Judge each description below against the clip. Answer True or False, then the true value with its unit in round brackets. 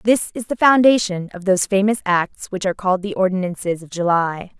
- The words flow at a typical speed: True (195 wpm)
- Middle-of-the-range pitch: False (195 Hz)